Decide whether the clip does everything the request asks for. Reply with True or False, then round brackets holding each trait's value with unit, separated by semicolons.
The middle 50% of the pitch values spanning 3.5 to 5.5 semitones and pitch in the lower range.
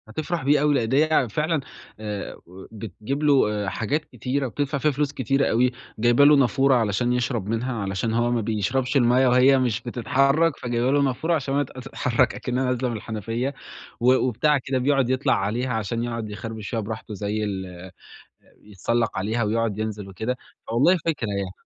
True (3.8 semitones; 120 Hz)